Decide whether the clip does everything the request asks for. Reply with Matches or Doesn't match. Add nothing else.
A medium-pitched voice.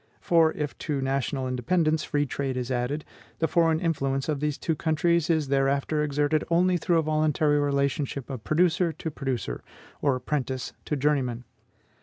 Matches